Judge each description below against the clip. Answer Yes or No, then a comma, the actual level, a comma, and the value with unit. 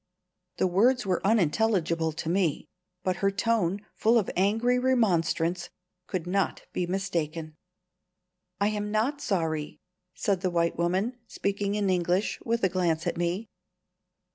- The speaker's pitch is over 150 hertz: Yes, high, 190 Hz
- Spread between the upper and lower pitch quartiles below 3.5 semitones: No, average, 3.8 semitones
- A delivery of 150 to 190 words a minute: No, average, 140 wpm